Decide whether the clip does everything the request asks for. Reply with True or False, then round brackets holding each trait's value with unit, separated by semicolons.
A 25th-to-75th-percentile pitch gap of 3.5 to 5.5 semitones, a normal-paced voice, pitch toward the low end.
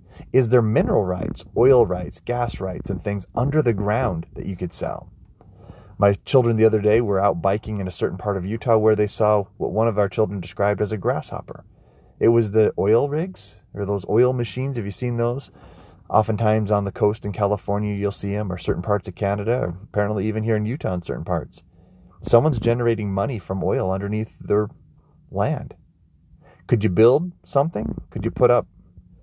False (2.8 semitones; 195 wpm; 105 Hz)